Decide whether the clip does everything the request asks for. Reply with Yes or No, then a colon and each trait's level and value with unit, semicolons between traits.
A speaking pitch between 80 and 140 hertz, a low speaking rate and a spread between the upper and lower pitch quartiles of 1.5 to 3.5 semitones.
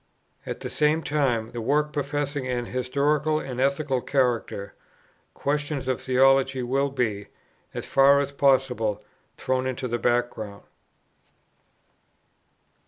Yes: low, 135 Hz; slow, 120 wpm; narrow, 2.6 semitones